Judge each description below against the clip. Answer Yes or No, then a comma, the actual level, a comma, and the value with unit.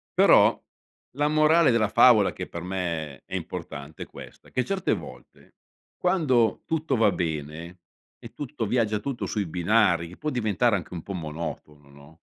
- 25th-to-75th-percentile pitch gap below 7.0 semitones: No, wide, 7.3 semitones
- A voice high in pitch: No, low, 105 Hz